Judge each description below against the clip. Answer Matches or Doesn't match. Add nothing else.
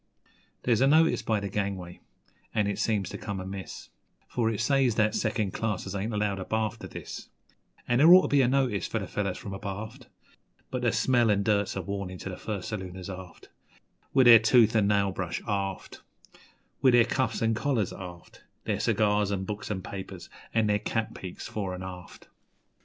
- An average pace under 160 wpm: Doesn't match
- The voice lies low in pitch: Matches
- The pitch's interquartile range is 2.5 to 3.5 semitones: Matches